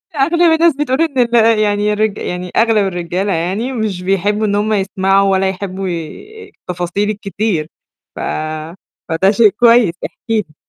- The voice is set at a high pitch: Yes, high, 205 Hz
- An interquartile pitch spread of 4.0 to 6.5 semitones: No, average, 3.3 semitones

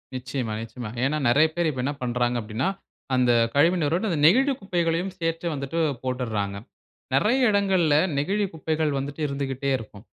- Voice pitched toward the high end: No, medium, 145 Hz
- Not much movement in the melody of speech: No, average, 5.3 semitones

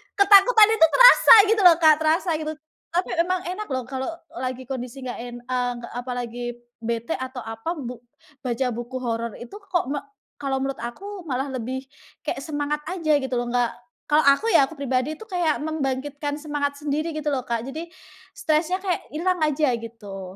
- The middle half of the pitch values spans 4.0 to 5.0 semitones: Yes, average, 4.5 semitones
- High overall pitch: Yes, very high, 280 Hz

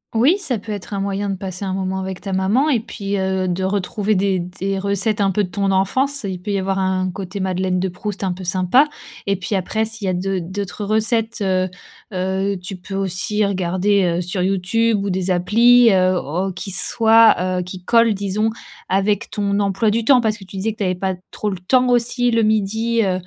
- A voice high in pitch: Yes, high, 195 Hz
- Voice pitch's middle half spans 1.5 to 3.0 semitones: Yes, narrow, 2.6 semitones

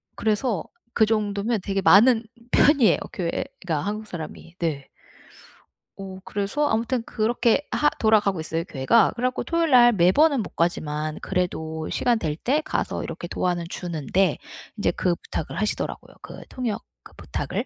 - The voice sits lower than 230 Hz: Yes, high, 200 Hz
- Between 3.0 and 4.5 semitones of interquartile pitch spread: No, wide, 5.6 semitones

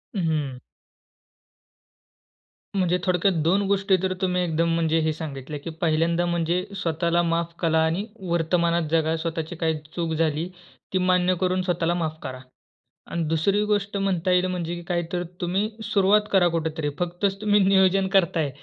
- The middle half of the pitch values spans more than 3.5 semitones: No, narrow, 2.4 semitones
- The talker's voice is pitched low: No, medium, 175 Hz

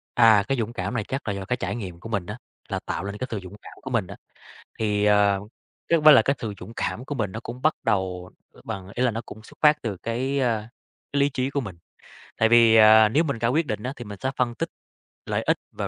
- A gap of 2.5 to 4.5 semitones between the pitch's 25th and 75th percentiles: Yes, average, 3.8 semitones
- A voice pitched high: No, low, 115 Hz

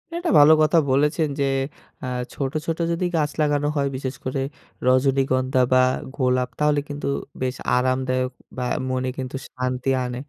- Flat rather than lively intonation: Yes, narrow, 2.3 semitones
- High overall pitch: No, low, 130 Hz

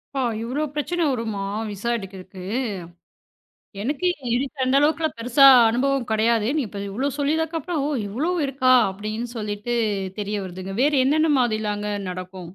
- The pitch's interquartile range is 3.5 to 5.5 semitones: Yes, average, 5.2 semitones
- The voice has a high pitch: Yes, high, 235 Hz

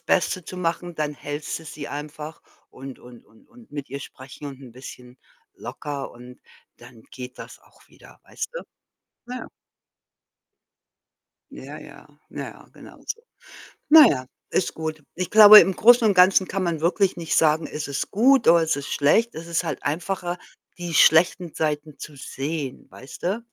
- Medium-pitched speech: Yes, medium, 160 Hz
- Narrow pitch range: No, average, 4.5 semitones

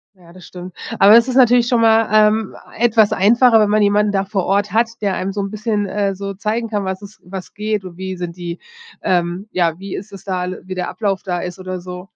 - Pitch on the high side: Yes, high, 200 Hz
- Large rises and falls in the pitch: No, average, 2.7 semitones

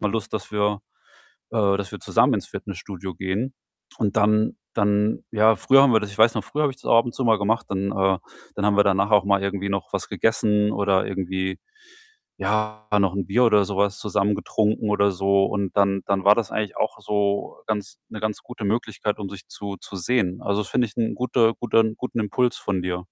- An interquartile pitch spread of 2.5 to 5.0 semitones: No, narrow, 1.9 semitones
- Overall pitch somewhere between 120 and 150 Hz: No, low, 105 Hz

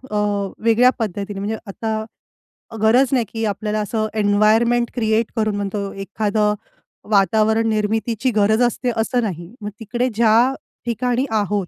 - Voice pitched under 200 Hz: No, high, 220 Hz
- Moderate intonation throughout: No, narrow, 2.0 semitones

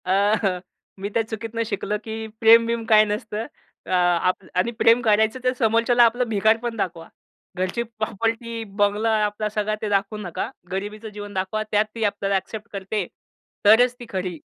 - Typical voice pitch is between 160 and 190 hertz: No, high, 215 Hz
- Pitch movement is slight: Yes, narrow, 2.2 semitones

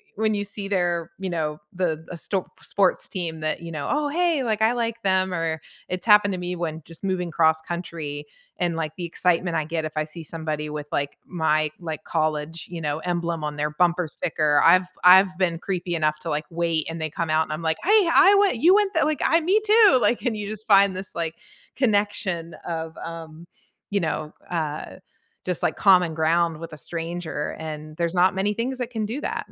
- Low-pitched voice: No, medium, 170 Hz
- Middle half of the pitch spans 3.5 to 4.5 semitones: Yes, average, 4.0 semitones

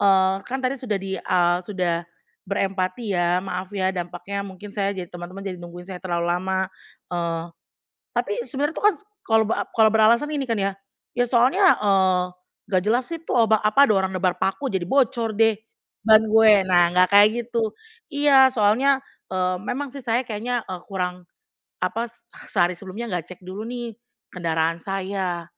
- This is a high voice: Yes, high, 195 Hz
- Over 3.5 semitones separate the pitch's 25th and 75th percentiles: Yes, average, 4.2 semitones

